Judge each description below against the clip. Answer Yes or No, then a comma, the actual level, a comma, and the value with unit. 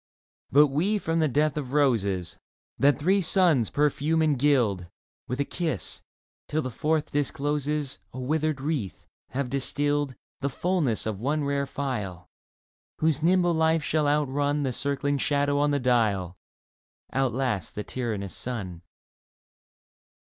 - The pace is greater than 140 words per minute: No, slow, 135 wpm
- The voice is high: No, medium, 140 Hz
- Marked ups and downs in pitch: No, average, 3.3 semitones